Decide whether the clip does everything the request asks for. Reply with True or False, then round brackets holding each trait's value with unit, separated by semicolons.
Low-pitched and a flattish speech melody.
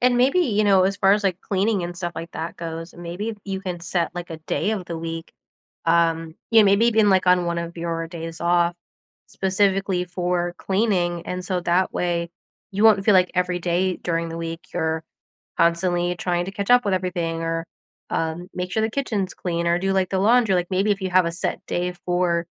False (180 Hz; 2.3 semitones)